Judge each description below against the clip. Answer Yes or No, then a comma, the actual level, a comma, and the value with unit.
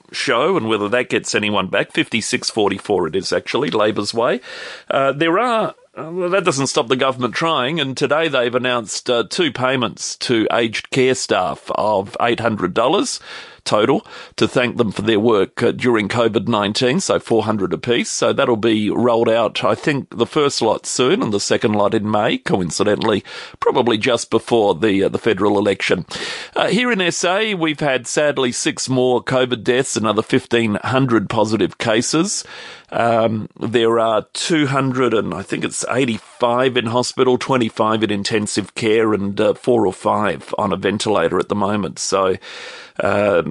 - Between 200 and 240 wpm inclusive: No, average, 180 wpm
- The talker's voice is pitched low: Yes, low, 125 Hz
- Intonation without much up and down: No, average, 3.5 semitones